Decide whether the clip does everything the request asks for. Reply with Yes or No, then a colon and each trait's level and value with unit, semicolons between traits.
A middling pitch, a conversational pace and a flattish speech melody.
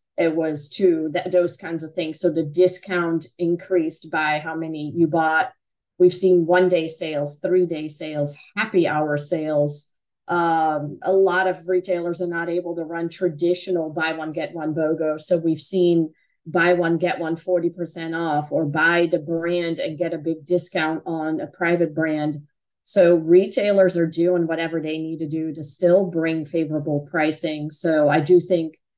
Yes: medium, 165 Hz; average, 175 wpm; narrow, 2.0 semitones